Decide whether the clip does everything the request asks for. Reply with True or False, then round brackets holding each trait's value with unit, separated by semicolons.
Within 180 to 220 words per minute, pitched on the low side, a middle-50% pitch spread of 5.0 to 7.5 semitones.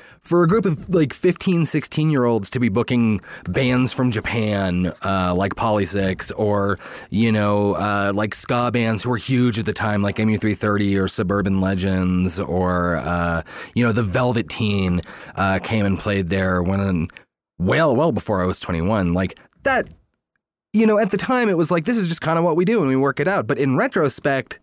True (200 wpm; 110 Hz; 5.5 semitones)